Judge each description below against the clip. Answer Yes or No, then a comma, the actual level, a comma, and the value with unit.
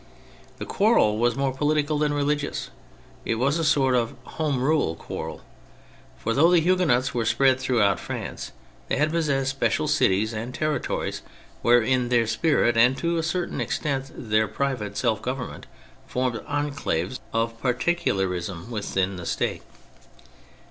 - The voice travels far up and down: No, average, 4.5 semitones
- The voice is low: Yes, low, 130 Hz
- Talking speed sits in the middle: Yes, average, 150 wpm